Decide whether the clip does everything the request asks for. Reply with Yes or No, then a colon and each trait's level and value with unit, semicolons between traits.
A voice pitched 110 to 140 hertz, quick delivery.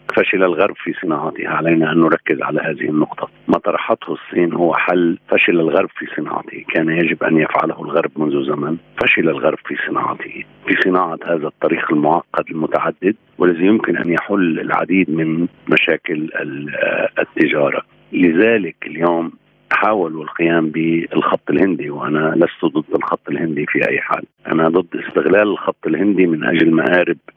No: very low, 85 Hz; fast, 145 wpm